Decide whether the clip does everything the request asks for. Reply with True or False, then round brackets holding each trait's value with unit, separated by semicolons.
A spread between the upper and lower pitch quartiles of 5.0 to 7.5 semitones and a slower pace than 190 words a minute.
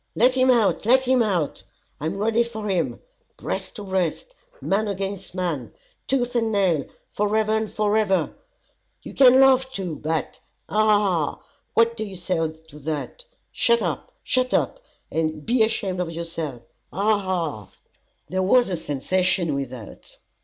True (5.4 semitones; 160 wpm)